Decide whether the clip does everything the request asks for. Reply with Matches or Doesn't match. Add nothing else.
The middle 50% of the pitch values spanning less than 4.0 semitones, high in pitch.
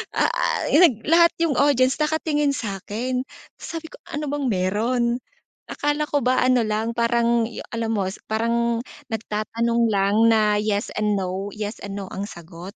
Doesn't match